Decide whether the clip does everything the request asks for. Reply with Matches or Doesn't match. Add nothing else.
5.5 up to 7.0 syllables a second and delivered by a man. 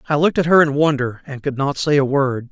Matches